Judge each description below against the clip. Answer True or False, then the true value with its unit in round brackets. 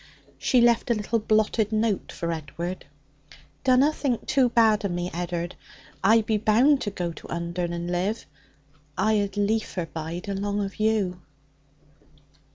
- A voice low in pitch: False (205 Hz)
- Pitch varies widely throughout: False (4.0 semitones)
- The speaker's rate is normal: True (150 wpm)